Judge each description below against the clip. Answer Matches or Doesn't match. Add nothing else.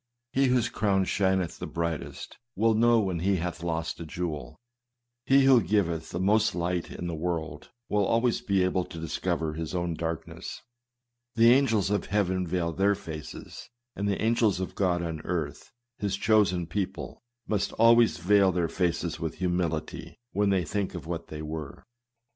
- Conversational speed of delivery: Matches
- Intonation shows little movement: Doesn't match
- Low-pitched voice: Matches